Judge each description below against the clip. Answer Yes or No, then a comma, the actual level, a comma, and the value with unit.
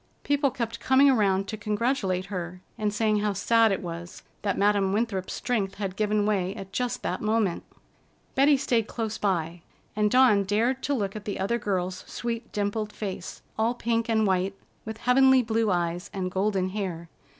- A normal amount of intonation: Yes, average, 3.1 semitones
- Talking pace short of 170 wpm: No, average, 175 wpm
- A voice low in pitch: No, high, 210 Hz